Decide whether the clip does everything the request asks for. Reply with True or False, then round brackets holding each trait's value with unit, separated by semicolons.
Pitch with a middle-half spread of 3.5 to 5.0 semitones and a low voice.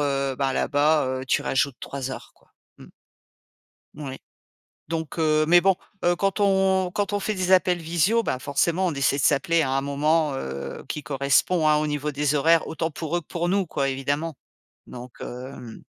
False (4.0 semitones; 150 Hz)